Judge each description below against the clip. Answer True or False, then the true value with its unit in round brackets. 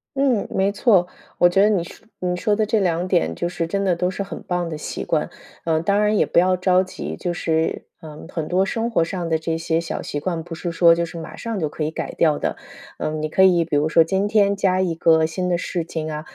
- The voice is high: False (175 Hz)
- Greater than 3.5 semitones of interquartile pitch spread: False (2.9 semitones)